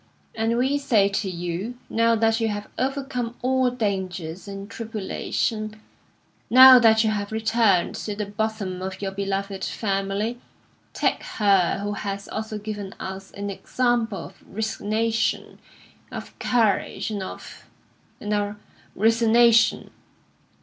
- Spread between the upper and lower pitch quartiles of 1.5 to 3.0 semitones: Yes, narrow, 2.6 semitones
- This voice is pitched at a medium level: No, high, 215 Hz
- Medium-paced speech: No, slow, 130 wpm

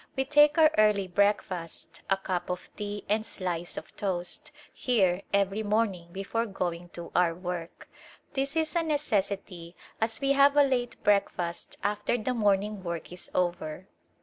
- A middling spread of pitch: Yes, average, 4.6 semitones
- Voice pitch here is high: Yes, high, 200 Hz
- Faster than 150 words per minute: Yes, average, 170 wpm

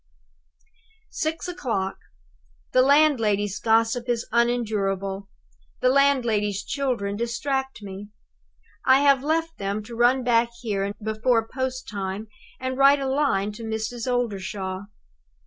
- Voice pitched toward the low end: No, high, 235 Hz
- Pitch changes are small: No, average, 4.3 semitones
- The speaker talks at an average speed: No, slow, 115 wpm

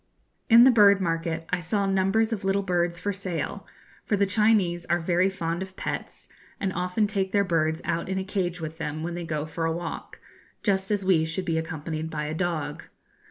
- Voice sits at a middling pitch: Yes, medium, 180 Hz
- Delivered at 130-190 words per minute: No, fast, 205 wpm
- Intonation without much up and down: No, average, 3.0 semitones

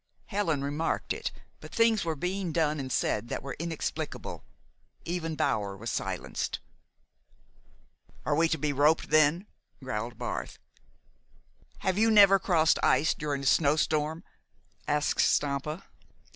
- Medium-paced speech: No, slow, 130 wpm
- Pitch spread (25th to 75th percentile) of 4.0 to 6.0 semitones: No, average, 3.4 semitones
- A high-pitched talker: No, medium, 155 Hz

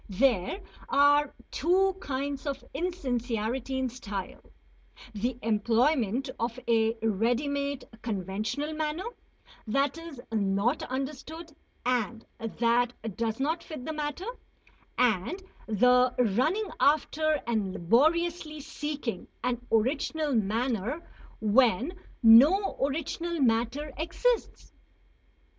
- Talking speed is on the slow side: Yes, slow, 100 wpm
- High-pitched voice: Yes, very high, 260 Hz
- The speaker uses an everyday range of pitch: Yes, average, 5.0 semitones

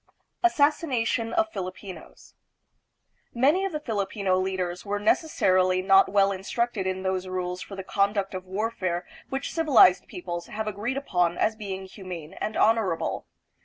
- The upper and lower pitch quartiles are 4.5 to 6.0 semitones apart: No, average, 3.5 semitones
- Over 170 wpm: No, average, 140 wpm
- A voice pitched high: Yes, high, 195 Hz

